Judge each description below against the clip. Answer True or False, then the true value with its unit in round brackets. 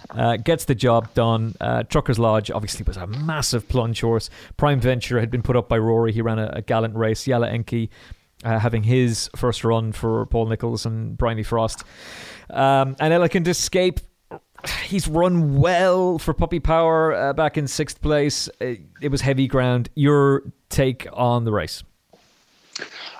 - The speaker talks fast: False (170 wpm)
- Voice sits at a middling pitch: False (125 Hz)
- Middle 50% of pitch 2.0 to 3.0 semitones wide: False (4.2 semitones)